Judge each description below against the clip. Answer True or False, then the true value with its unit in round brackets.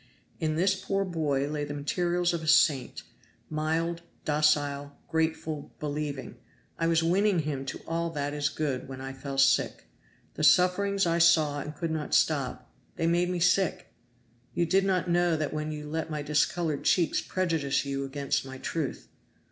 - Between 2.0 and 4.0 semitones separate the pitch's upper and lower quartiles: True (3.0 semitones)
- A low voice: False (155 Hz)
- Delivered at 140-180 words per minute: True (170 wpm)